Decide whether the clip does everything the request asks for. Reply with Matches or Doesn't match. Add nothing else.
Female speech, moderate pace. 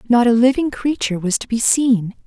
Doesn't match